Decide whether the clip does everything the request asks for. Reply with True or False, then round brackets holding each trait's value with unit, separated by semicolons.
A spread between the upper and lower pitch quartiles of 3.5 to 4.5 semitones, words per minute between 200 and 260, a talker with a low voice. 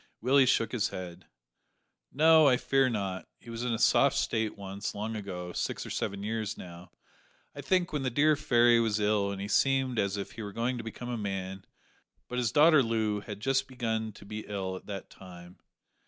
True (3.9 semitones; 205 wpm; 110 Hz)